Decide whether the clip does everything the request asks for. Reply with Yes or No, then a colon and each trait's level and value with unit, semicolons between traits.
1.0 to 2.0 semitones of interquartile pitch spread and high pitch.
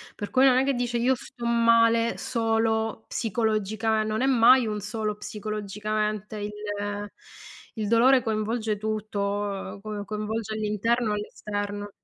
Yes: narrow, 1.7 semitones; high, 215 Hz